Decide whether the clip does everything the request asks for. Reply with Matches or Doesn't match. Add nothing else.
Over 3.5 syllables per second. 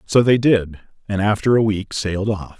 Matches